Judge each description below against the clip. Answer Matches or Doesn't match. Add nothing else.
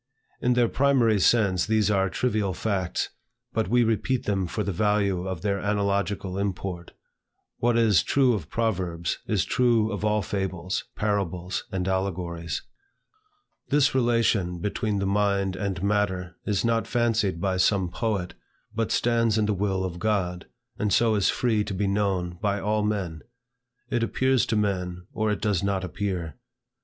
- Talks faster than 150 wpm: Matches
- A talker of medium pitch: Doesn't match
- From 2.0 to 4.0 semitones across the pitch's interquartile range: Matches